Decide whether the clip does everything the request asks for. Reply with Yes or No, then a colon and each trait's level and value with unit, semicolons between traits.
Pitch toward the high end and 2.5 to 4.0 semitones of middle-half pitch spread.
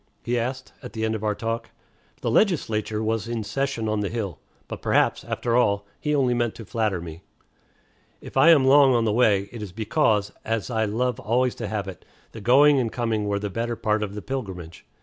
No: low, 115 Hz; average, 2.9 semitones